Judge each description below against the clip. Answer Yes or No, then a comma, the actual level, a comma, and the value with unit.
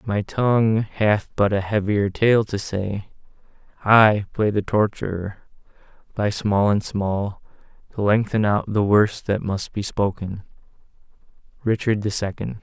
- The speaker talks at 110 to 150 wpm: Yes, average, 140 wpm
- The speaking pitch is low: Yes, low, 105 Hz